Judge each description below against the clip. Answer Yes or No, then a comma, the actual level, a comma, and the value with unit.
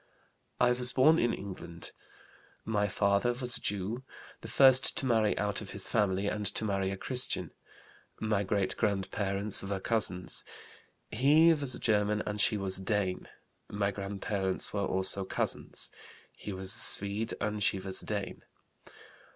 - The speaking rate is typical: Yes, average, 160 wpm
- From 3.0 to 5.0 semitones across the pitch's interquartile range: No, narrow, 2.5 semitones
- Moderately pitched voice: No, low, 105 Hz